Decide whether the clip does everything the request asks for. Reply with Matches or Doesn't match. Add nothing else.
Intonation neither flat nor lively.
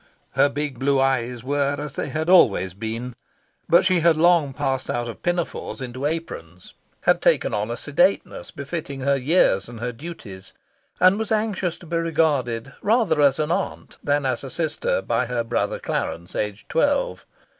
Doesn't match